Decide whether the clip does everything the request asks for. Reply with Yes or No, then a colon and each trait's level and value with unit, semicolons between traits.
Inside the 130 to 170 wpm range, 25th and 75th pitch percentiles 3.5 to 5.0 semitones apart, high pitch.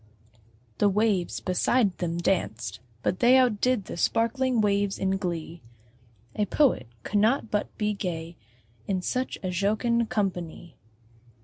Yes: slow, 135 wpm; average, 4.2 semitones; high, 200 Hz